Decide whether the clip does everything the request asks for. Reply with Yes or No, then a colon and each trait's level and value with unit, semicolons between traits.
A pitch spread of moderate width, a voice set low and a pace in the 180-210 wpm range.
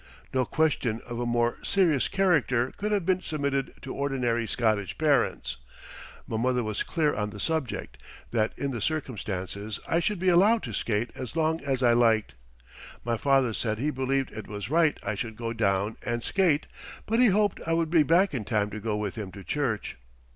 No: wide, 6.2 semitones; low, 125 Hz; average, 195 wpm